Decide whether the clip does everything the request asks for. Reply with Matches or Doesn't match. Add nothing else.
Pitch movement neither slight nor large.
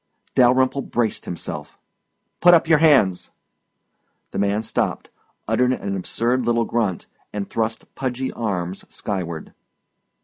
Matches